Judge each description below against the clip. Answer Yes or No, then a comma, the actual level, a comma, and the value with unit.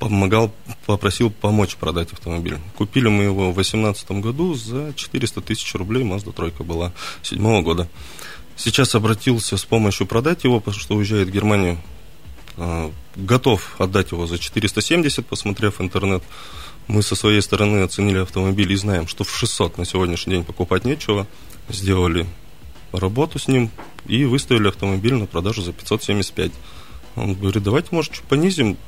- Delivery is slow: No, average, 150 wpm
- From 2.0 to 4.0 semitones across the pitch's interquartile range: Yes, average, 3.7 semitones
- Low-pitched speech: Yes, low, 100 Hz